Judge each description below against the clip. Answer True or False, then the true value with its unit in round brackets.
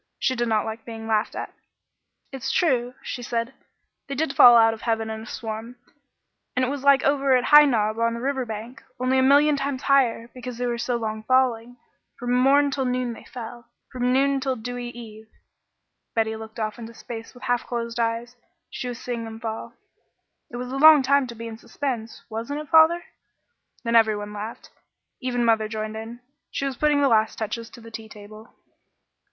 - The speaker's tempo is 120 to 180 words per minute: False (200 wpm)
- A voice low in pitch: False (240 Hz)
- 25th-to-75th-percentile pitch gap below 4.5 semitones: True (2.7 semitones)